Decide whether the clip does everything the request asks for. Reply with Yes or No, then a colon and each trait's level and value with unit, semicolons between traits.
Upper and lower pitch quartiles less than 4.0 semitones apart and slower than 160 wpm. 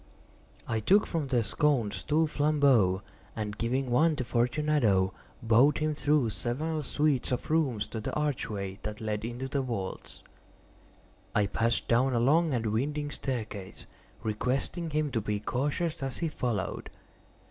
No: average, 5.3 semitones; average, 145 wpm